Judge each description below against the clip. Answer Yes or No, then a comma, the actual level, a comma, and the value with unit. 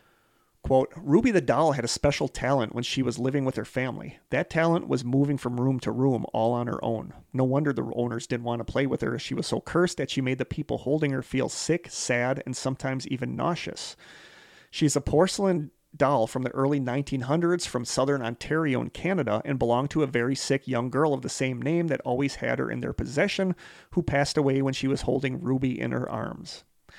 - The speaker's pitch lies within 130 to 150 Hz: Yes, low, 135 Hz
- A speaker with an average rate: No, fast, 220 wpm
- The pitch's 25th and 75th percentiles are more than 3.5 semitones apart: No, narrow, 2.6 semitones